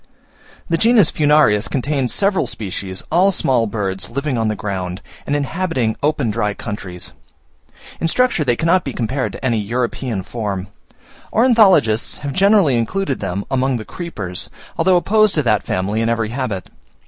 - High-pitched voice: No, low, 125 Hz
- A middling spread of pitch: No, wide, 7.5 semitones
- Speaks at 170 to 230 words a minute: No, average, 155 wpm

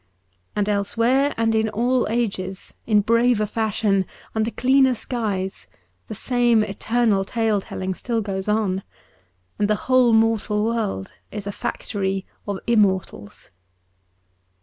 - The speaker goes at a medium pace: No, slow, 125 wpm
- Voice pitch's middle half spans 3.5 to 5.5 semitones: No, average, 2.8 semitones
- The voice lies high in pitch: Yes, high, 215 Hz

